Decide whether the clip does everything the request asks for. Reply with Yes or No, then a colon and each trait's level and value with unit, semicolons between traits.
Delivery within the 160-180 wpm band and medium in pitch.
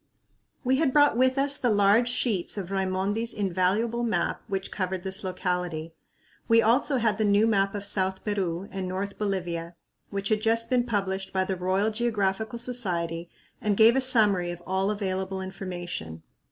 No: average, 165 wpm; high, 200 Hz